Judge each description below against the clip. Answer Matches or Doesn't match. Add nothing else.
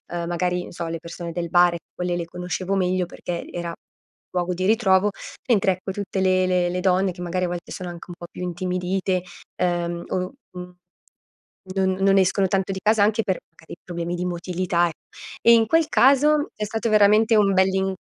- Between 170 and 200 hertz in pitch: Matches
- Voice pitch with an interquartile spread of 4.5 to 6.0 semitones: Doesn't match